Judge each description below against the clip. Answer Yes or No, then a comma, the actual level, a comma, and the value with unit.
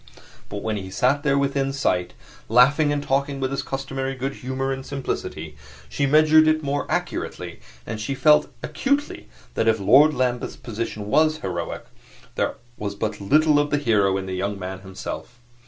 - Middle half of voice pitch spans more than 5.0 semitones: Yes, wide, 5.4 semitones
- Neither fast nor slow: Yes, average, 170 wpm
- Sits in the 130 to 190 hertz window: Yes, low, 135 Hz